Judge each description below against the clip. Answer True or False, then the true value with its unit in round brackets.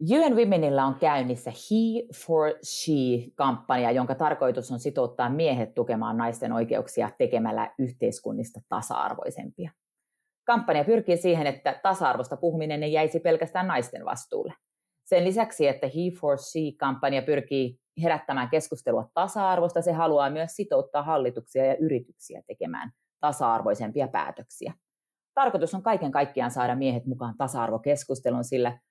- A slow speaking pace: True (120 wpm)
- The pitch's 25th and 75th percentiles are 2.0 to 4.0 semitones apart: False (5.1 semitones)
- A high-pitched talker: False (150 Hz)